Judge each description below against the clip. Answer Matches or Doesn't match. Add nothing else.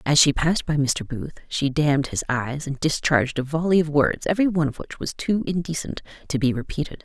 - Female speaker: Matches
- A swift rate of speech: Matches